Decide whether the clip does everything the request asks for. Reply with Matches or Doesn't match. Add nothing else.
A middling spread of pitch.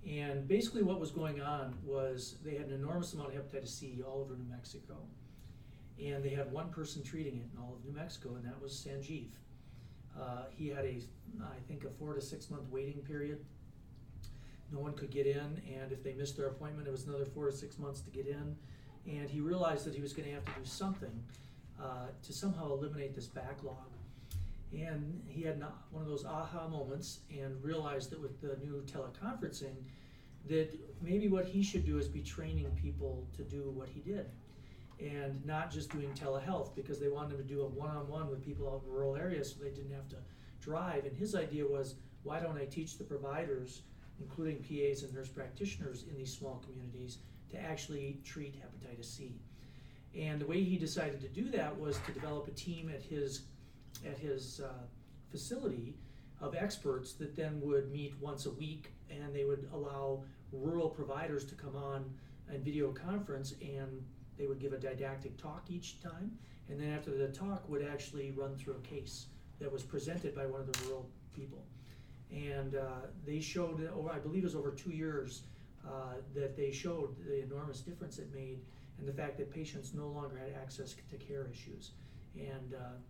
Doesn't match